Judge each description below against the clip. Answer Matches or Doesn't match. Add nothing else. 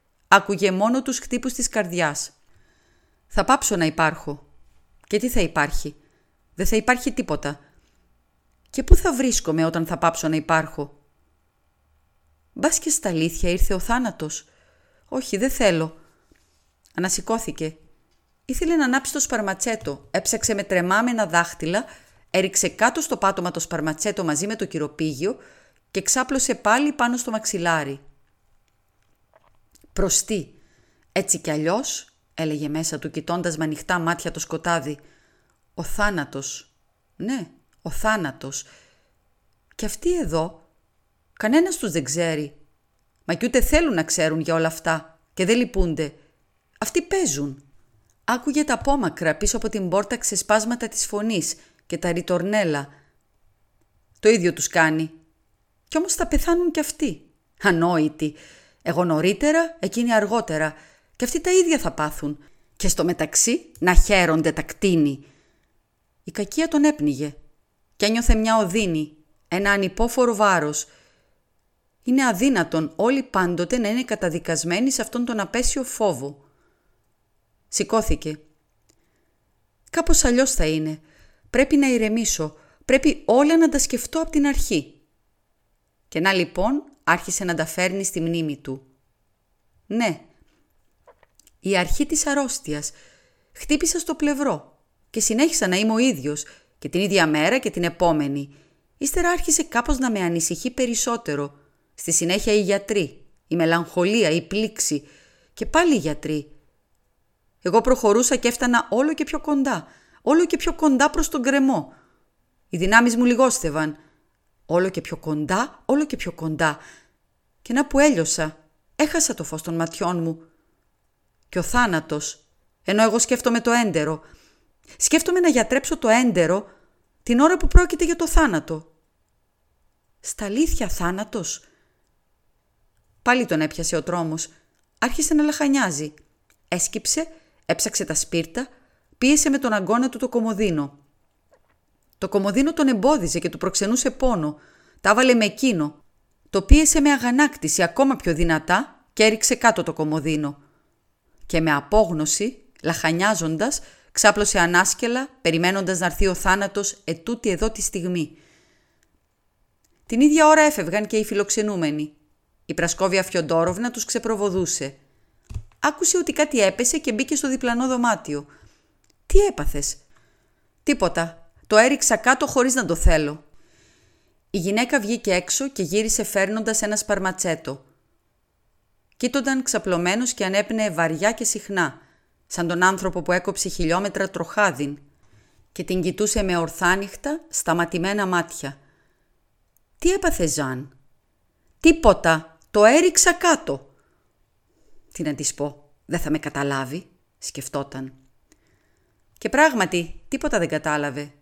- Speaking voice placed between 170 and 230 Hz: Matches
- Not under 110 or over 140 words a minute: Matches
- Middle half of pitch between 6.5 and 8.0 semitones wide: Matches